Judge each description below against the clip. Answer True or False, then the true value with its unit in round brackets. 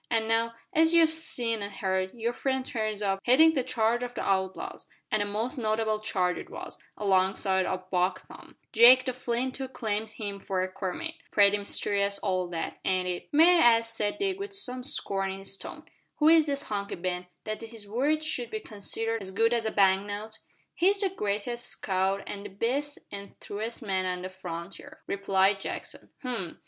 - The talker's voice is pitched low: False (215 Hz)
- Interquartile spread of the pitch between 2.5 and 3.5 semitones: False (4.4 semitones)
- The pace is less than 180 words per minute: False (195 wpm)